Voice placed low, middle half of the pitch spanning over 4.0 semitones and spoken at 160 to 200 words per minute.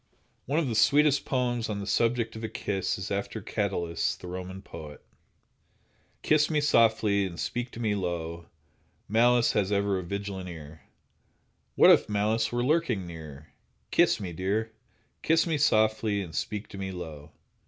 Yes: low, 105 Hz; average, 4.5 semitones; average, 165 wpm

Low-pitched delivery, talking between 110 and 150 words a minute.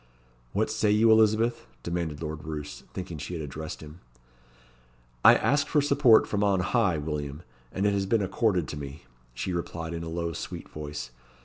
No: very low, 85 Hz; average, 180 wpm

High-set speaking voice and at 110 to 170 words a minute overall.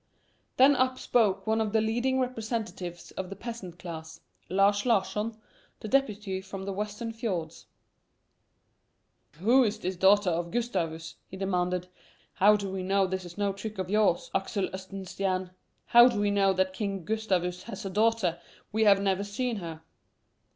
Yes: high, 200 Hz; average, 160 wpm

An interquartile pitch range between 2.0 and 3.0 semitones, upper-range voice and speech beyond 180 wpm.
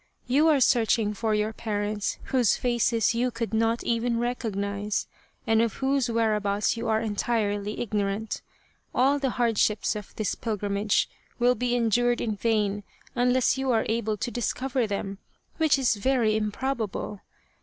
No: average, 2.7 semitones; high, 225 Hz; average, 155 wpm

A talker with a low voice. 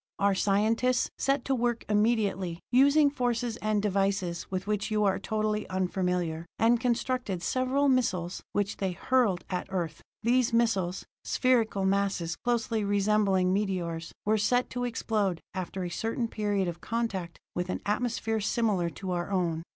No: high, 205 Hz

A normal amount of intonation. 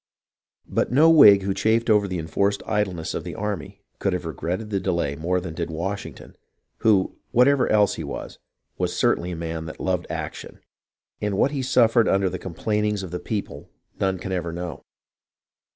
Yes: average, 3.5 semitones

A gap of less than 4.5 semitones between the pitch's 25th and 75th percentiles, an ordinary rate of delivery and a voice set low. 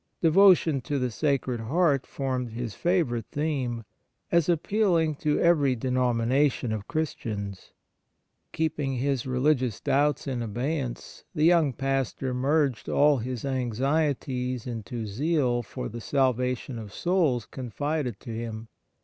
Yes: average, 3.9 semitones; average, 145 wpm; low, 130 Hz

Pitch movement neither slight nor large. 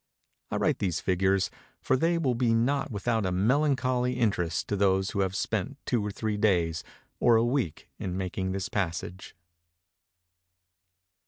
Yes: average, 4.7 semitones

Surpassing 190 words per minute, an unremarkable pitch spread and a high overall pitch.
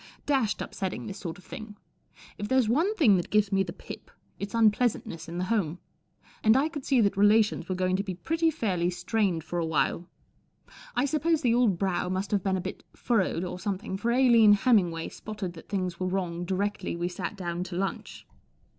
Yes: average, 200 wpm; average, 4.1 semitones; high, 200 Hz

